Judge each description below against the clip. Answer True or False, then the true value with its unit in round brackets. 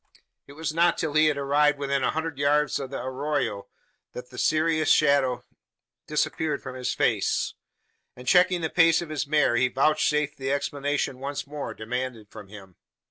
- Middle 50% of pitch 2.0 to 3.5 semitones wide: True (2.9 semitones)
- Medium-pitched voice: True (145 Hz)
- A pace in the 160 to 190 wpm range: True (175 wpm)